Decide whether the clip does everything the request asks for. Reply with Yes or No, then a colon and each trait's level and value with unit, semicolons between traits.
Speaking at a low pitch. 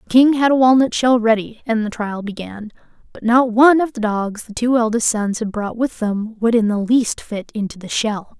No: high, 225 Hz